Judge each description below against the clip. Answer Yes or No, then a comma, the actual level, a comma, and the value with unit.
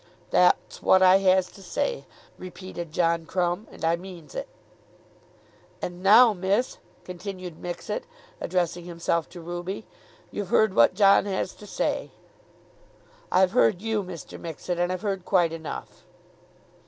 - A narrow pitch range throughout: Yes, narrow, 2.1 semitones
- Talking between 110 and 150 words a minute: Yes, average, 140 wpm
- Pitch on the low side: No, medium, 185 Hz